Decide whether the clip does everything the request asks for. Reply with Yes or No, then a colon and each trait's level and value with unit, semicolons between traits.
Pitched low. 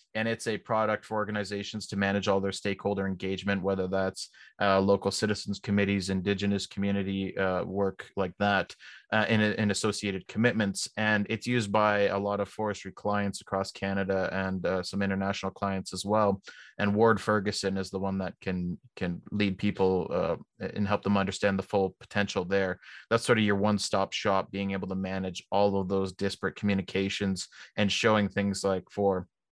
Yes: low, 100 Hz